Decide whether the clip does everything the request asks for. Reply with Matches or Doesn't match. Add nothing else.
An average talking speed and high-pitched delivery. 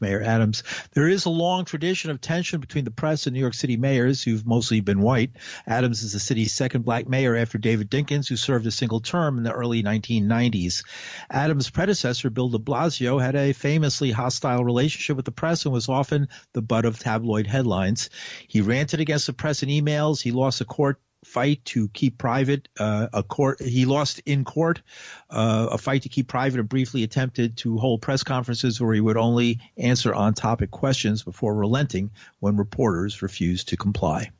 Doesn't match